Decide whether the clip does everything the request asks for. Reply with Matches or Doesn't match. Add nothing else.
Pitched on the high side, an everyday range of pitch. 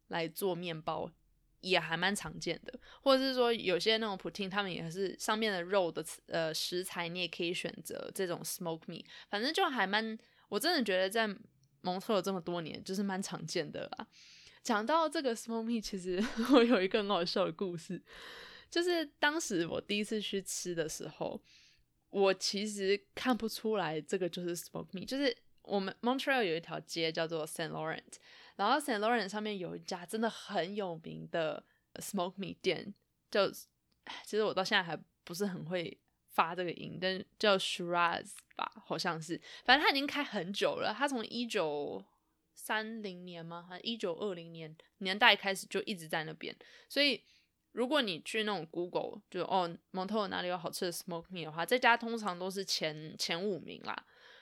Matches